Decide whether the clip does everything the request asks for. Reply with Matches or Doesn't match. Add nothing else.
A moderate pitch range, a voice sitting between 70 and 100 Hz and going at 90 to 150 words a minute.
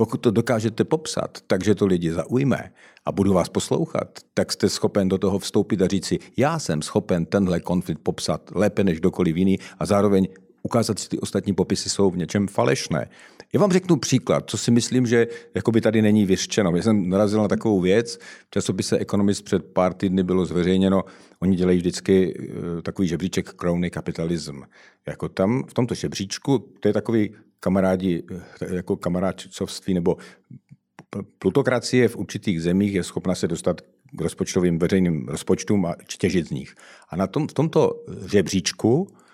Doesn't match